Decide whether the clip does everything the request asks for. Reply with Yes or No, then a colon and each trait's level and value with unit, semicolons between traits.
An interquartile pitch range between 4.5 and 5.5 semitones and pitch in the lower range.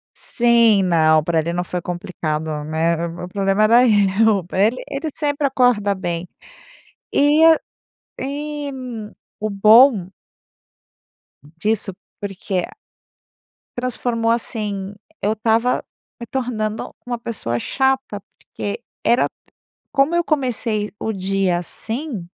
No: average, 4.9 semitones; high, 210 Hz